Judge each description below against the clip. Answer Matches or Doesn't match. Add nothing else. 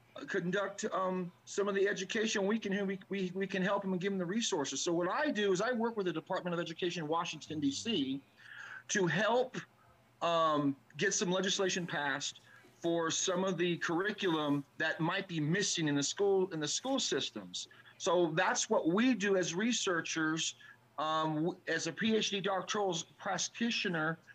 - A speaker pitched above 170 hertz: Matches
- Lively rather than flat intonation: Doesn't match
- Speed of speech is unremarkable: Doesn't match